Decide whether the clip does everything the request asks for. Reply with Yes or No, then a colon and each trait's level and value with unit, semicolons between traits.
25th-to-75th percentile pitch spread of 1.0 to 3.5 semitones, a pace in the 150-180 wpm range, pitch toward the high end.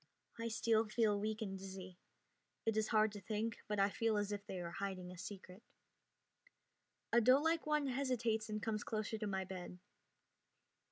Yes: average, 2.7 semitones; average, 170 wpm; high, 215 Hz